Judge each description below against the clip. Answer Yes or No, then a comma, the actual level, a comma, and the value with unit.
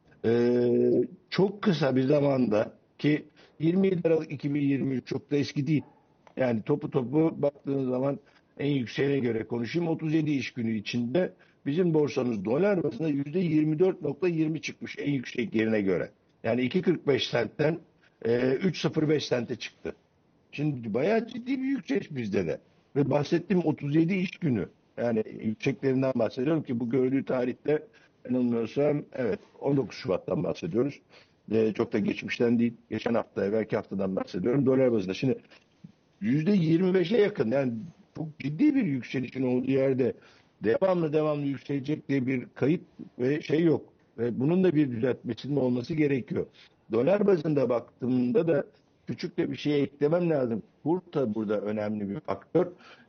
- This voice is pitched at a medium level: Yes, medium, 145 Hz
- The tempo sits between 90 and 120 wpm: No, average, 135 wpm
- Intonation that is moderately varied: Yes, average, 4.4 semitones